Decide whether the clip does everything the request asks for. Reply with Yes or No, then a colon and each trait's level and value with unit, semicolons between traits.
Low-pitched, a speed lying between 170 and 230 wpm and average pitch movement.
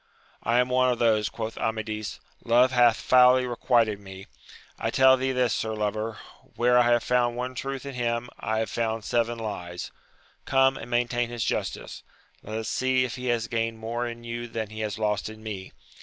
No: low, 120 Hz; average, 195 wpm; narrow, 2.1 semitones